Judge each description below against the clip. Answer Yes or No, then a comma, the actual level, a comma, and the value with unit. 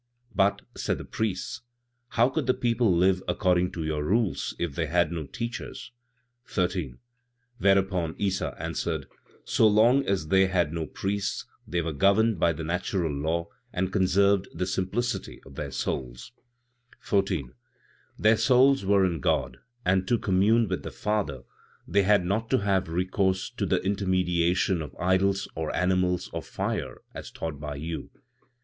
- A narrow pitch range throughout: No, average, 3.1 semitones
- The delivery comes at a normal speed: Yes, average, 155 wpm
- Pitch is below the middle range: Yes, very low, 95 Hz